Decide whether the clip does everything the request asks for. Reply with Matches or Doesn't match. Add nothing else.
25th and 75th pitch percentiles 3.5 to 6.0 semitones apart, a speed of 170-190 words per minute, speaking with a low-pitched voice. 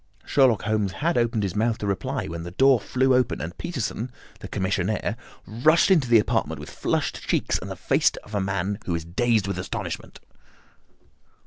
Matches